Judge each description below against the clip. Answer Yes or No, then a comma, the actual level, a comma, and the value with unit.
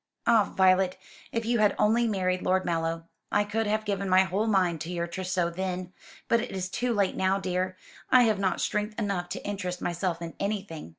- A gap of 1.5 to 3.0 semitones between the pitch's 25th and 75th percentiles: Yes, narrow, 2.6 semitones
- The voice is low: No, high, 190 Hz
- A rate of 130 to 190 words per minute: No, average, 200 wpm